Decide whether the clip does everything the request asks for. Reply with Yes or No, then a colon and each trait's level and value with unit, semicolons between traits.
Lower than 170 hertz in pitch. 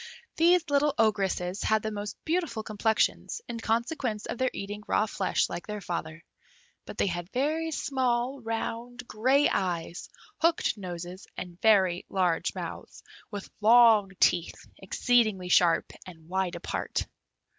No: high, 215 Hz